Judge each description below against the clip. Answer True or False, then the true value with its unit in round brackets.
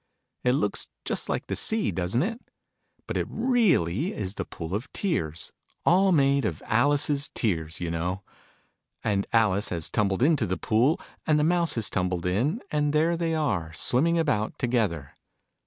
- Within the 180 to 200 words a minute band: False (165 wpm)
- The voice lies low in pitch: True (120 Hz)